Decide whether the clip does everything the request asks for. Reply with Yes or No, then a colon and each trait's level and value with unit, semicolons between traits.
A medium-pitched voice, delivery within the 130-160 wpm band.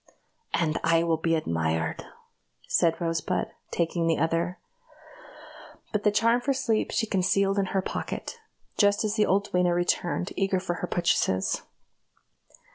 Yes: medium, 180 Hz; average, 140 wpm